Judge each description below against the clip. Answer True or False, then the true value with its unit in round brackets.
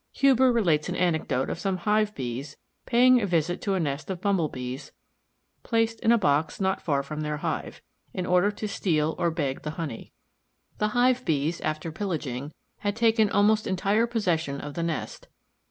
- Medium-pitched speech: True (175 Hz)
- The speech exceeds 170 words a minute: True (180 wpm)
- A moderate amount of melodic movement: False (5.8 semitones)